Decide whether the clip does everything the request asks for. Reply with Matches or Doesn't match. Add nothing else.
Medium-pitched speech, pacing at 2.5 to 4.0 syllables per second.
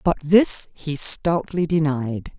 Matches